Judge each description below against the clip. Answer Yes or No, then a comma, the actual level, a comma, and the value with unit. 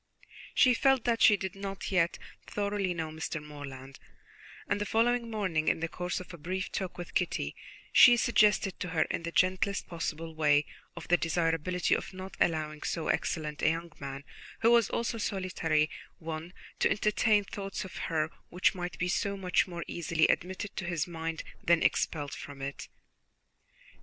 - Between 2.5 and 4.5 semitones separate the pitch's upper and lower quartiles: Yes, average, 3.7 semitones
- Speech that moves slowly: No, average, 175 wpm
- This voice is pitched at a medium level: Yes, medium, 175 Hz